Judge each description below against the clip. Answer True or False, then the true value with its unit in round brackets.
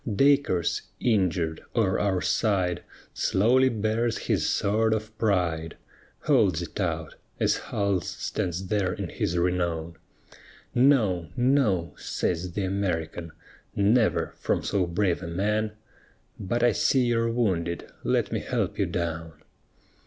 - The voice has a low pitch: True (95 Hz)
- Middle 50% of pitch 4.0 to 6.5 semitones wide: True (4.4 semitones)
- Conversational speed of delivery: False (125 wpm)